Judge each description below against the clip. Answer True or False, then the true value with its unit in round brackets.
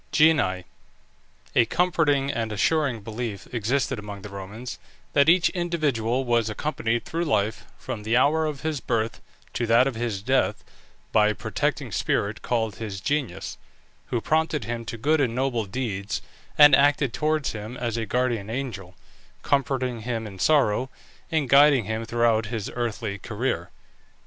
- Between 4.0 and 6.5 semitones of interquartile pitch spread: True (4.4 semitones)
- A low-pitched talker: True (120 Hz)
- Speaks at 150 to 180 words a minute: True (155 wpm)